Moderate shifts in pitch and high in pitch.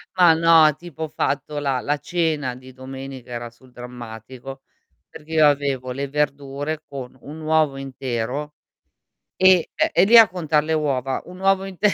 No: average, 3.4 semitones; medium, 145 Hz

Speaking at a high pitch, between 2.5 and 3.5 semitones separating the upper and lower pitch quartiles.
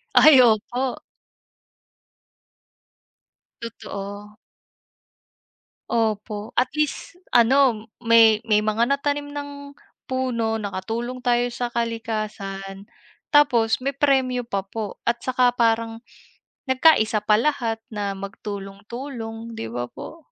Yes: high, 230 Hz; average, 3.2 semitones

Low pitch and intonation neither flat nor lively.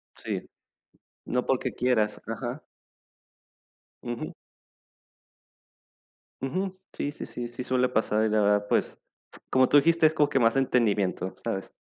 Yes: low, 125 Hz; average, 3.8 semitones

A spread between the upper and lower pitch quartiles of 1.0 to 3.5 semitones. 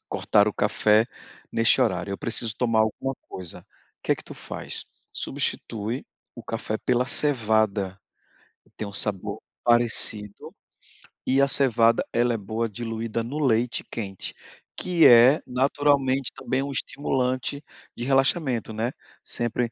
Yes: average, 3.2 semitones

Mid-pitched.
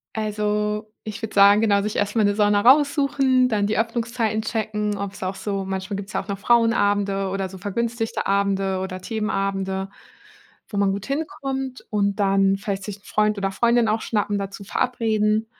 No: high, 210 Hz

